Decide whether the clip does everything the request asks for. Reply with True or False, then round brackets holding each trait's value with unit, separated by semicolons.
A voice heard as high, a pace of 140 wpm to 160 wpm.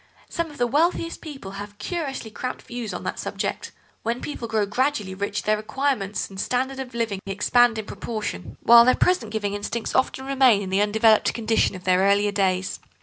False (220 Hz; 190 wpm)